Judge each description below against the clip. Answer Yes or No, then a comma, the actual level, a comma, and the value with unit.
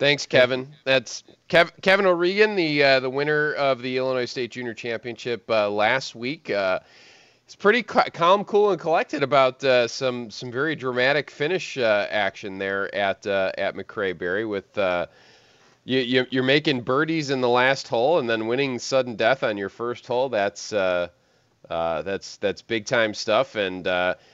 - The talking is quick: No, average, 175 wpm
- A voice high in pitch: No, low, 130 Hz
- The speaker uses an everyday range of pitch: Yes, average, 3.8 semitones